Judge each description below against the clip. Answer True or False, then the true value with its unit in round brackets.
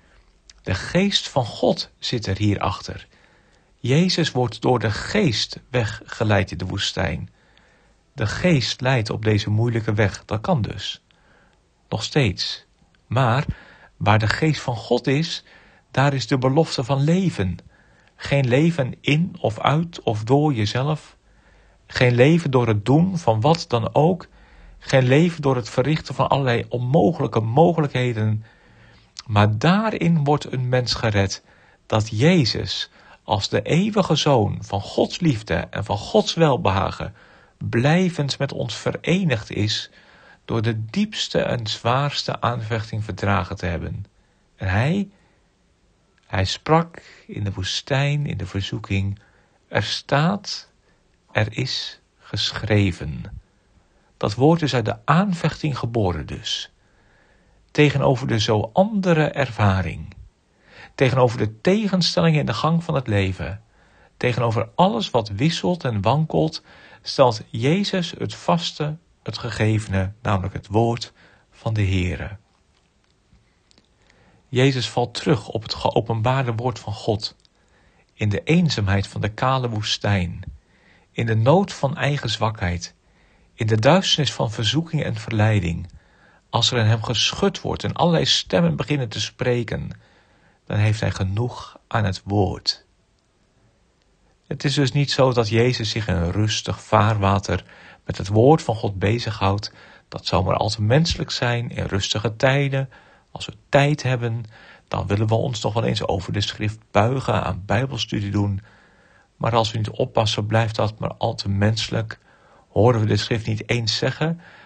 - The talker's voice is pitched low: True (115 Hz)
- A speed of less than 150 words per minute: True (140 wpm)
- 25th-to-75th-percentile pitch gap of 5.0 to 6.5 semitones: True (5.5 semitones)